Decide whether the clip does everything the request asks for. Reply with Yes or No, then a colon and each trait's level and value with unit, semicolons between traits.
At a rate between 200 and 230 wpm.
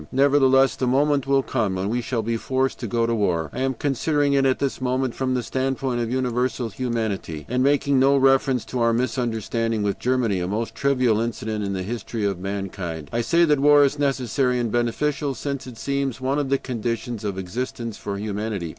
Yes: fast, 205 wpm